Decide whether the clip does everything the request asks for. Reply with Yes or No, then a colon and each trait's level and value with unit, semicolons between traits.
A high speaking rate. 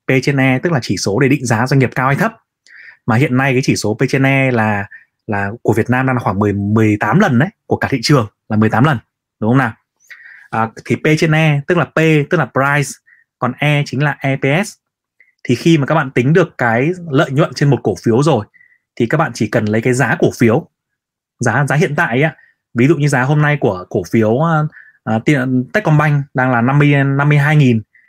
No: average, 210 wpm